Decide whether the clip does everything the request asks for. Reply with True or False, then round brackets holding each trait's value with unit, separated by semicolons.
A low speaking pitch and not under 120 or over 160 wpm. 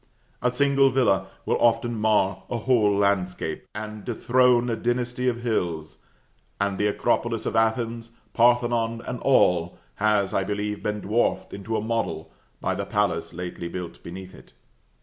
True (110 Hz; 150 wpm)